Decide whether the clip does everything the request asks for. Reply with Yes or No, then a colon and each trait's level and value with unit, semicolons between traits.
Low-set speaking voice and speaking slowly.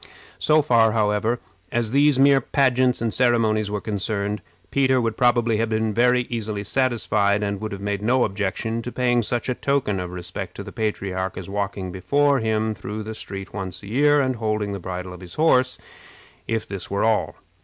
No: low, 110 Hz; average, 190 wpm